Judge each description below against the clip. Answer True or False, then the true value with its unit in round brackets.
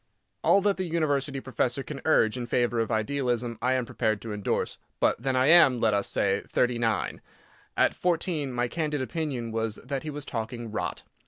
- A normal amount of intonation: True (4.2 semitones)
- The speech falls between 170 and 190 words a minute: True (185 wpm)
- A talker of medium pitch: False (125 Hz)